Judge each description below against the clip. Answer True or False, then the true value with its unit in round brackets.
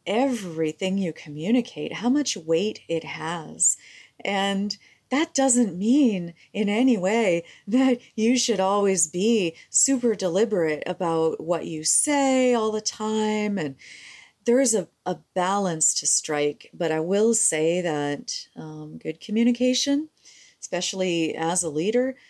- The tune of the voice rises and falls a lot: True (6.6 semitones)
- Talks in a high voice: True (200 Hz)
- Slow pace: True (130 wpm)